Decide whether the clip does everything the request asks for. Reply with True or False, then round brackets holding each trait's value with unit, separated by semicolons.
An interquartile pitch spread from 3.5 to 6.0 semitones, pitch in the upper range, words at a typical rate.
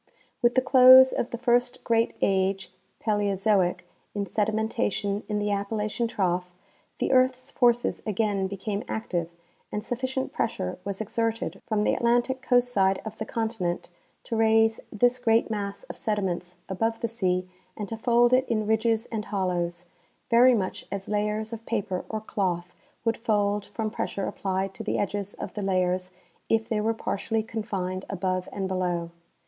False (3.1 semitones; 210 Hz; 165 wpm)